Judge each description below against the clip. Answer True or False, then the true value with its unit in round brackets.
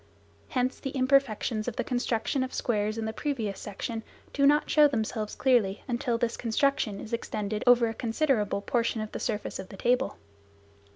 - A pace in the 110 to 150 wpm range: False (175 wpm)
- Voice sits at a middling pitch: False (235 Hz)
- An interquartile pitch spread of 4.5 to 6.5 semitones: False (3.2 semitones)